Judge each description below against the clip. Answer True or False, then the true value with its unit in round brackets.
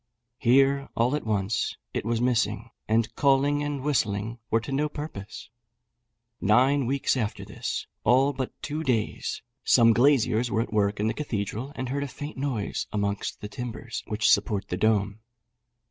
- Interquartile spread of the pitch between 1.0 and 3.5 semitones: False (4.4 semitones)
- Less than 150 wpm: False (160 wpm)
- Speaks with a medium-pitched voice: False (115 Hz)